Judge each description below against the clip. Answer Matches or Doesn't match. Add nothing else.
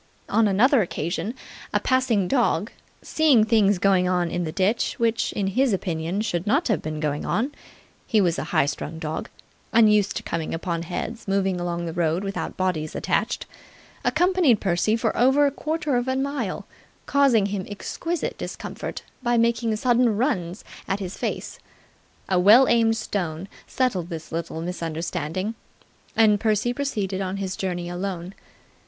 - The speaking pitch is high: Matches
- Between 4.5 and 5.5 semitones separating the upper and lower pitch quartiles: Matches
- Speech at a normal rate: Matches